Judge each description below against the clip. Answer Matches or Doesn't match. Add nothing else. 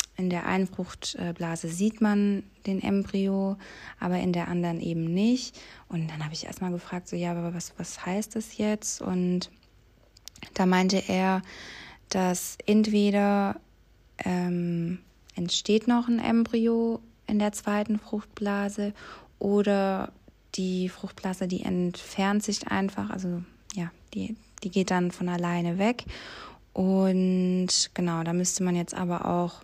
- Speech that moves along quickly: Doesn't match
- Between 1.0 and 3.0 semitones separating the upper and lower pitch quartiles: Matches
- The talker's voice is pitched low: Doesn't match